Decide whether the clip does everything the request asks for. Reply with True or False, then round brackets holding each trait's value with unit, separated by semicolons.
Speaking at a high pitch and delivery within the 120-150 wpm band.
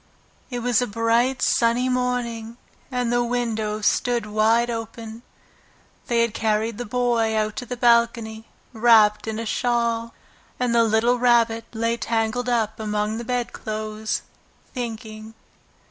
True (230 Hz; 140 wpm)